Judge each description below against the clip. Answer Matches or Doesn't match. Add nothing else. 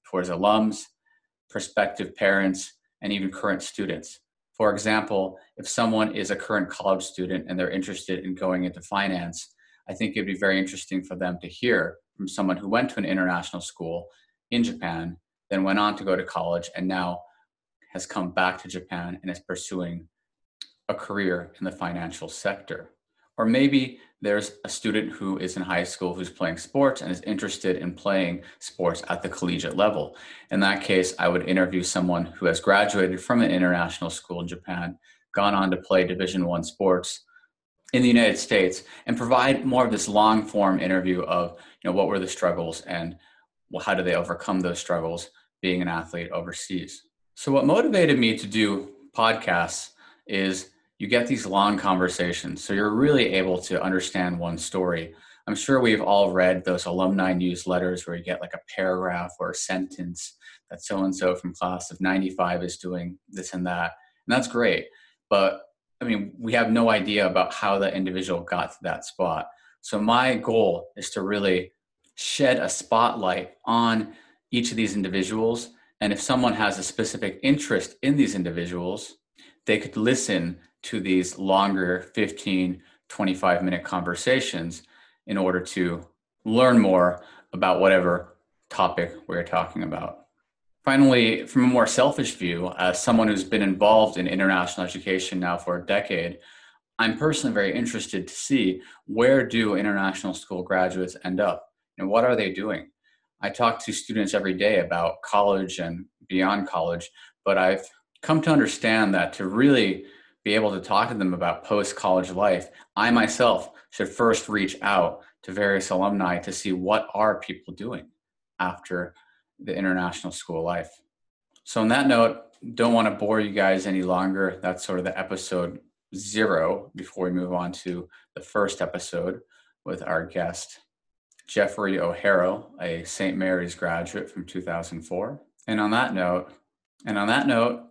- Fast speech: Doesn't match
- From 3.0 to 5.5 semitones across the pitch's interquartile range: Doesn't match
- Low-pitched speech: Matches